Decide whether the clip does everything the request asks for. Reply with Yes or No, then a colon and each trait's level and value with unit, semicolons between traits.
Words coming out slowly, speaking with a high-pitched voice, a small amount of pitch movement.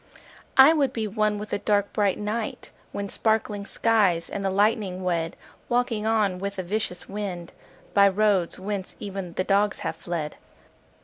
No: average, 165 wpm; high, 200 Hz; narrow, 2.3 semitones